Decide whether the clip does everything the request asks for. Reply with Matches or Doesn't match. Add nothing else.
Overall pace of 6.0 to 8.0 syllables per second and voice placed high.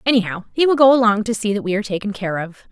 Matches